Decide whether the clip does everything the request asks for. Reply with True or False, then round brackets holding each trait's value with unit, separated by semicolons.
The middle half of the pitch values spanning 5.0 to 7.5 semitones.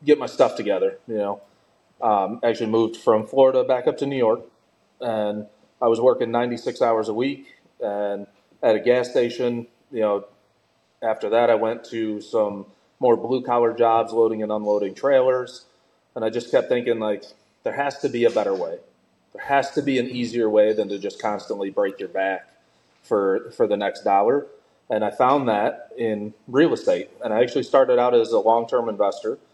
False (4.5 semitones)